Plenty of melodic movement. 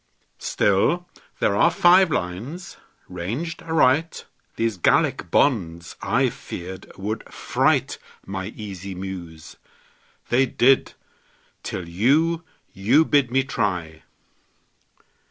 Yes: wide, 8.0 semitones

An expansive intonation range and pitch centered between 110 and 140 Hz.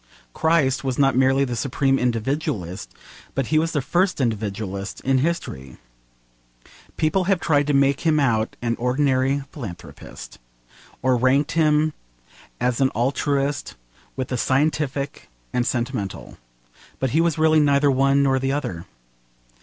No: average, 3.2 semitones; low, 135 Hz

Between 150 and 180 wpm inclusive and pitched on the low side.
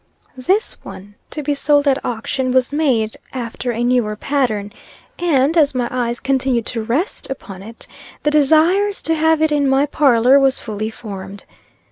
No: average, 165 wpm; very high, 265 Hz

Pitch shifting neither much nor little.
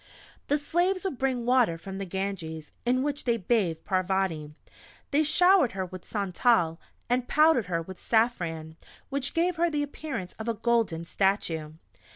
No: wide, 7.7 semitones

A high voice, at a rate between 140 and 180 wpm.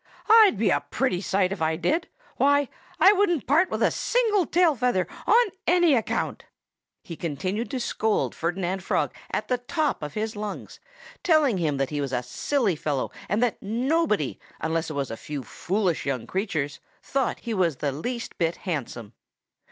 Yes: high, 205 Hz; average, 175 wpm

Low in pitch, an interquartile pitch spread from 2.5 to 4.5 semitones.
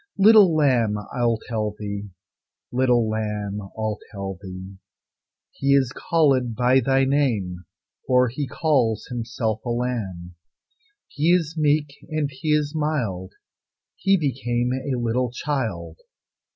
No: low, 125 Hz; average, 4.9 semitones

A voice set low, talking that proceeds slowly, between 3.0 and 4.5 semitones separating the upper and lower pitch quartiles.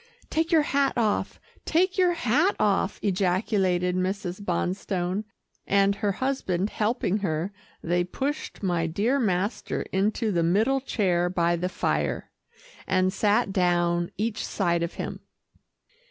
No: high, 195 Hz; slow, 130 wpm; average, 4.1 semitones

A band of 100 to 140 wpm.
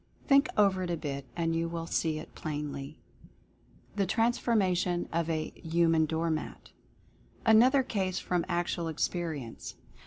Yes: slow, 135 wpm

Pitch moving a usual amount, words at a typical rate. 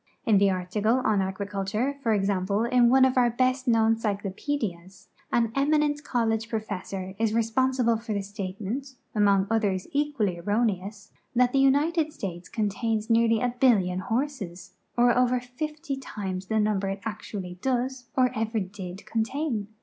Yes: average, 4.2 semitones; average, 150 wpm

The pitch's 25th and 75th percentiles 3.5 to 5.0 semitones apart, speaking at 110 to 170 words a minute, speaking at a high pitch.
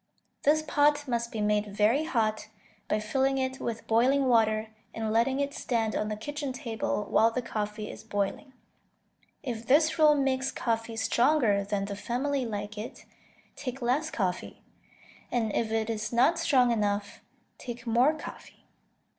Yes: average, 3.9 semitones; average, 155 wpm; high, 235 Hz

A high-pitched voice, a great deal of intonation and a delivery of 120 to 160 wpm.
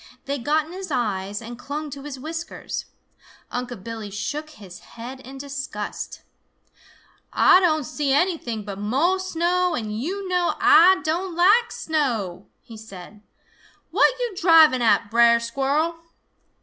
Yes: very high, 280 Hz; wide, 6.6 semitones; average, 140 wpm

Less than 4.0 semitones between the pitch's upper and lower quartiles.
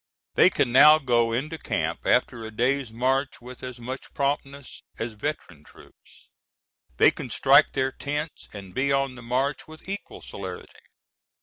Yes: average, 3.1 semitones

